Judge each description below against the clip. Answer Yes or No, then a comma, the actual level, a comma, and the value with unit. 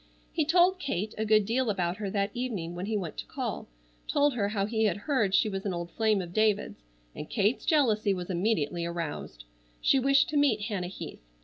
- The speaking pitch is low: No, high, 210 Hz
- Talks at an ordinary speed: No, fast, 210 wpm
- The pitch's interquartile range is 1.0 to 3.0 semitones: No, average, 4.5 semitones